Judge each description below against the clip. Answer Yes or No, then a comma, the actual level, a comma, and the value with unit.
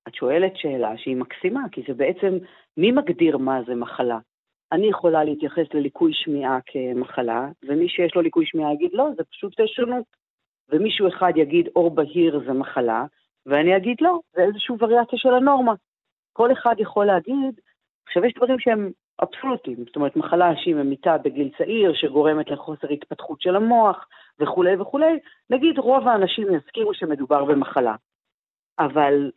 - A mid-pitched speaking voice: Yes, medium, 175 Hz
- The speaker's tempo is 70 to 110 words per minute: No, fast, 150 wpm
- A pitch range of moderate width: No, wide, 8.6 semitones